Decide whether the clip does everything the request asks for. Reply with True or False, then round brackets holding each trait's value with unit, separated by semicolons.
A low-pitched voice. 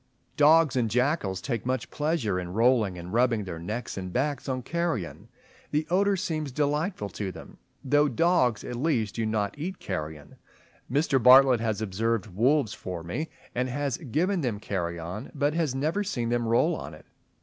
True (125 Hz)